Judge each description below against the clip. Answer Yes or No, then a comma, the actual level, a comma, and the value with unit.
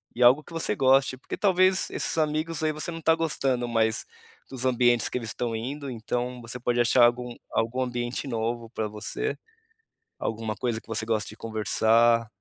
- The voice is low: Yes, low, 120 Hz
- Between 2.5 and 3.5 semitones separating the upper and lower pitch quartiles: Yes, average, 3.2 semitones